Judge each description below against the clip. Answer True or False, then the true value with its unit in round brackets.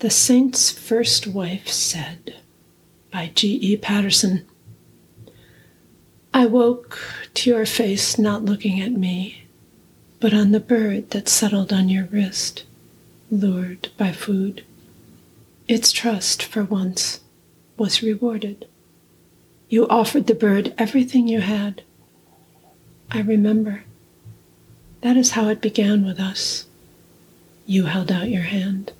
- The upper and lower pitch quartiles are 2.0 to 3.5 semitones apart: True (3.0 semitones)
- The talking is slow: True (115 wpm)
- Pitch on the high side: True (210 Hz)